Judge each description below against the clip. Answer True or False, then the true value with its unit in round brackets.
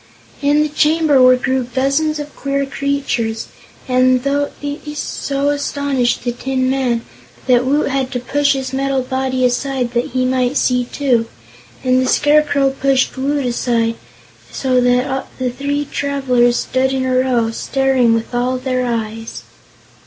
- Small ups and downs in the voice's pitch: True (2.0 semitones)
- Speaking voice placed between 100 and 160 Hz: False (260 Hz)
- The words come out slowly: False (150 wpm)